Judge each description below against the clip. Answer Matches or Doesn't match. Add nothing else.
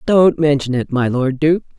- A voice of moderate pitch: Matches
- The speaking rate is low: Doesn't match